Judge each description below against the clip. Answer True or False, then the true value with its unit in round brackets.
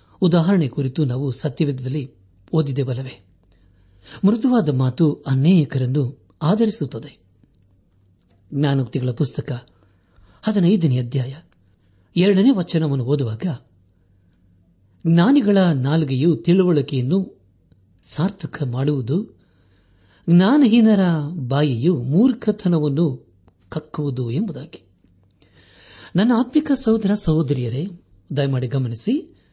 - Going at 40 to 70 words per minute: True (65 wpm)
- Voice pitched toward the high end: False (140 Hz)